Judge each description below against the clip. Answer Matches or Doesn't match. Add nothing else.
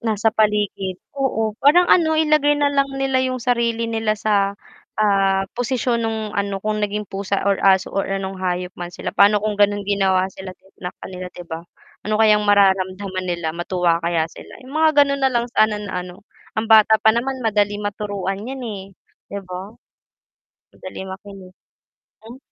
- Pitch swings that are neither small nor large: Matches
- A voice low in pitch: Doesn't match